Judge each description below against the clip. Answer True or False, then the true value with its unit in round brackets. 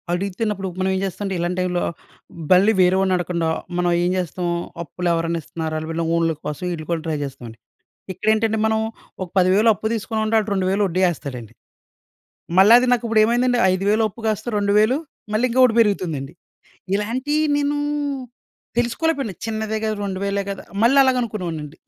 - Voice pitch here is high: True (195 Hz)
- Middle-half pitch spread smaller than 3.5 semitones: False (4.1 semitones)